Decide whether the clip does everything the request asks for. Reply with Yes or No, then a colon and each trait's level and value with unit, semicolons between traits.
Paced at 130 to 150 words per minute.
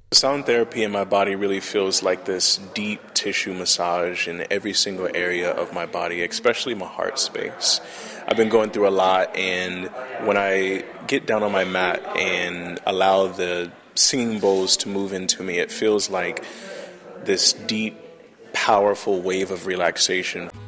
No: average, 165 wpm